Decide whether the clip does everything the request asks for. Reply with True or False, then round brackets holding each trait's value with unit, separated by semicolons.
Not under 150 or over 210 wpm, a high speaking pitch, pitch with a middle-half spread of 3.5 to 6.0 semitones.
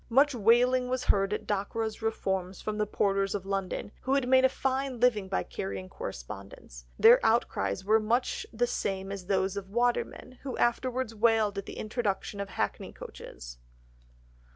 True (170 wpm; 210 Hz; 4.0 semitones)